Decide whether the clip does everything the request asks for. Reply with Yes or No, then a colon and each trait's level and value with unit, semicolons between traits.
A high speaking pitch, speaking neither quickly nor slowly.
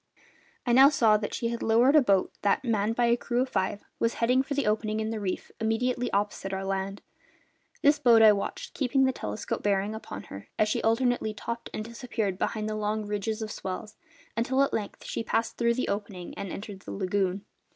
No: high, 220 Hz; fast, 210 wpm